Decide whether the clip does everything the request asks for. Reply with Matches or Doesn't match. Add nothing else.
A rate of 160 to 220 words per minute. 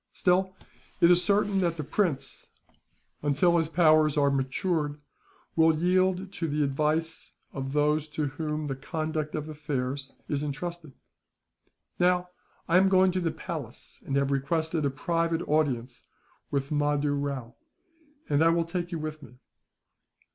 Doesn't match